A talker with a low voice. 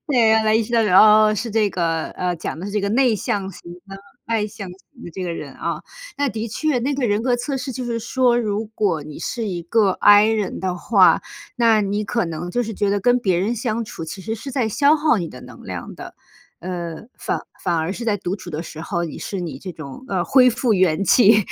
No: high, 210 Hz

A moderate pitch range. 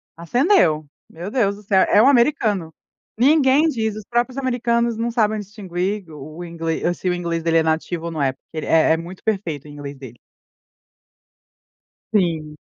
No: wide, 6.1 semitones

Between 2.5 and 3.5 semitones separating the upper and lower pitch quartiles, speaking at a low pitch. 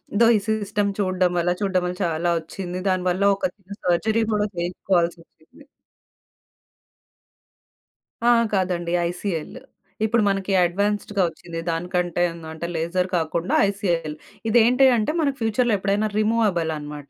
No: average, 3.2 semitones; medium, 185 Hz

